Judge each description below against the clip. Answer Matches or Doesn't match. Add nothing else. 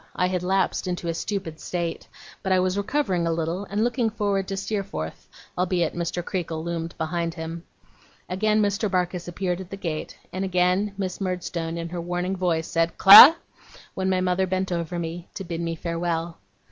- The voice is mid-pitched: Matches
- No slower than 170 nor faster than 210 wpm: Matches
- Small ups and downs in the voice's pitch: Matches